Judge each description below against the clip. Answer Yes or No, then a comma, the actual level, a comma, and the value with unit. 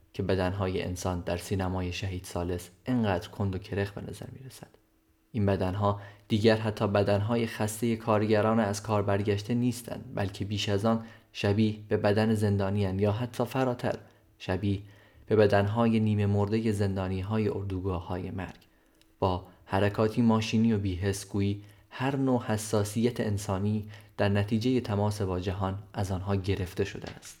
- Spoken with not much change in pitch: Yes, narrow, 2.2 semitones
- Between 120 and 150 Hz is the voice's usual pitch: No, low, 105 Hz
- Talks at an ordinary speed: Yes, average, 140 wpm